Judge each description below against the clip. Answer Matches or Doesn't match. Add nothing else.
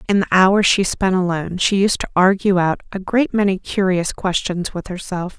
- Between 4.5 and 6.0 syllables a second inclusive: Matches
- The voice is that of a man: Doesn't match